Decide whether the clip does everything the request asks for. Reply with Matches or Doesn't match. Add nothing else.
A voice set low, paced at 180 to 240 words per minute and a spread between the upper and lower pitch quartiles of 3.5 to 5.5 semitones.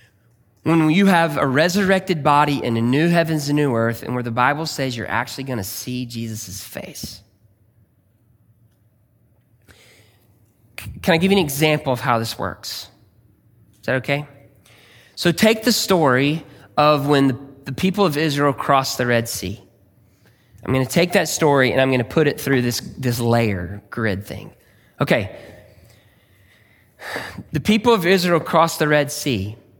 Doesn't match